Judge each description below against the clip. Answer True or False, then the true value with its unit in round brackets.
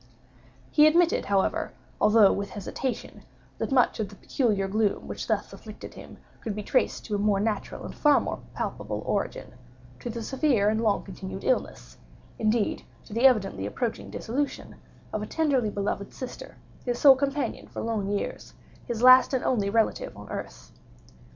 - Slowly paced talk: False (150 wpm)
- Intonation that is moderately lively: True (4.2 semitones)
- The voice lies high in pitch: True (225 Hz)